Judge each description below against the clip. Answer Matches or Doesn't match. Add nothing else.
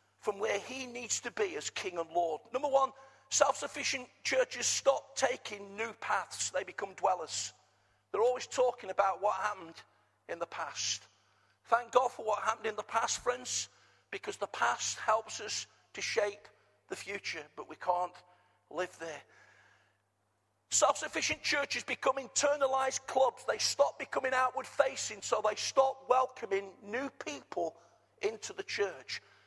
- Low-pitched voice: Doesn't match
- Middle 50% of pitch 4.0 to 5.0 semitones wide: Doesn't match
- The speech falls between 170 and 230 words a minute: Doesn't match